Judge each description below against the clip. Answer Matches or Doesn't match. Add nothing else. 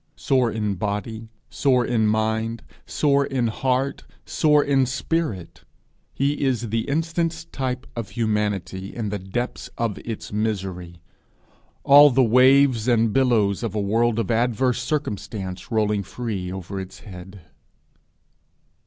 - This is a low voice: Matches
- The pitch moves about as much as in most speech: Matches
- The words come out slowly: Matches